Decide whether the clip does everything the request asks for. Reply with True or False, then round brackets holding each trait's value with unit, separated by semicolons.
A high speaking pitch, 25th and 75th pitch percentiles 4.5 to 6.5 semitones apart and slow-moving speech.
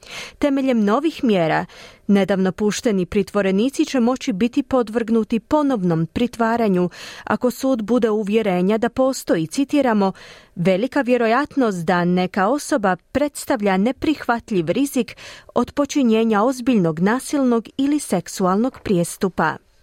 True (230 Hz; 5.3 semitones; 105 wpm)